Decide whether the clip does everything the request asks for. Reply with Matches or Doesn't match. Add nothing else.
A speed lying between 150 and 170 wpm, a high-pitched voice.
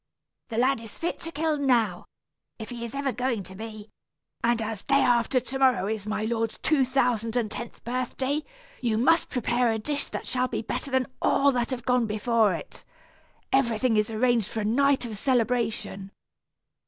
Doesn't match